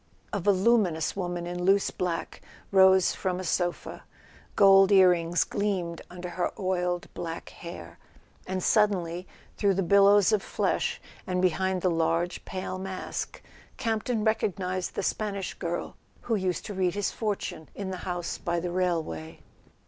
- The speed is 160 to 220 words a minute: No, average, 150 wpm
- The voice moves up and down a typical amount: No, narrow, 2.1 semitones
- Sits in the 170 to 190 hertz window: Yes, medium, 185 Hz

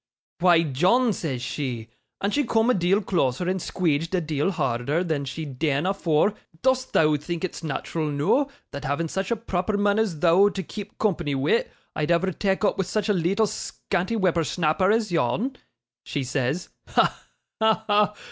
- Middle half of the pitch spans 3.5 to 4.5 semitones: No, average, 5.2 semitones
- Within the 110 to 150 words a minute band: No, average, 180 wpm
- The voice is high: No, medium, 175 Hz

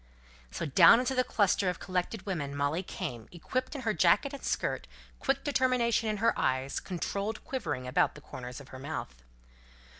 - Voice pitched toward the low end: No, medium, 185 Hz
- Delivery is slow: No, average, 175 wpm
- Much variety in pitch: Yes, wide, 8.7 semitones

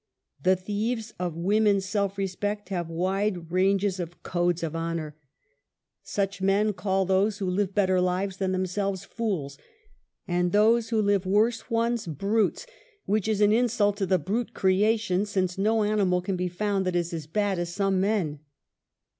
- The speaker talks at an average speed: Yes, average, 170 wpm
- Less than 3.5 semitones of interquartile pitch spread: Yes, narrow, 2.6 semitones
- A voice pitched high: Yes, high, 195 Hz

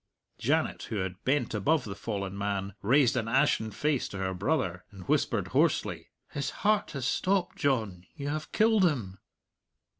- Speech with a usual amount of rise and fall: No, wide, 7.1 semitones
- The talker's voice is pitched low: Yes, low, 115 Hz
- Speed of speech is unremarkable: Yes, average, 160 wpm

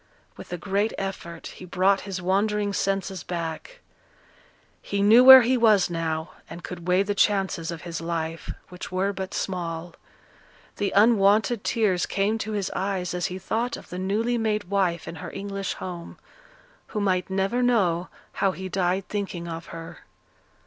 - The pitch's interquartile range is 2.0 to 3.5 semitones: Yes, narrow, 2.6 semitones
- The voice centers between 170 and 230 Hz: Yes, high, 190 Hz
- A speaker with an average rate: Yes, average, 165 wpm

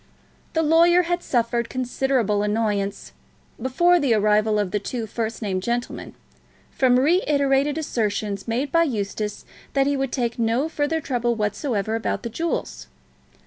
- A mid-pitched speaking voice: No, high, 240 Hz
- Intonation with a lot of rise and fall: No, average, 4.9 semitones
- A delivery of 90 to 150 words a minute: Yes, average, 145 wpm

